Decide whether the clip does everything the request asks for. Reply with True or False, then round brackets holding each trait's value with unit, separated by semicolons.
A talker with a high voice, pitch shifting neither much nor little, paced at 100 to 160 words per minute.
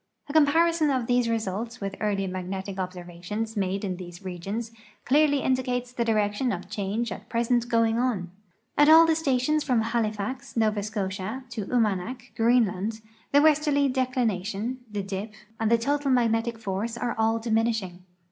True (225 Hz; 4.1 semitones; 155 wpm)